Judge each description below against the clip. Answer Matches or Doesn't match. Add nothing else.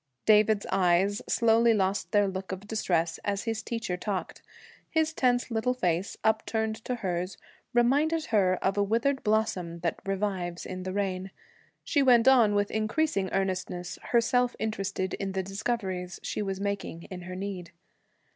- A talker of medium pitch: Doesn't match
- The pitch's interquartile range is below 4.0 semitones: Matches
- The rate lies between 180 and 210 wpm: Doesn't match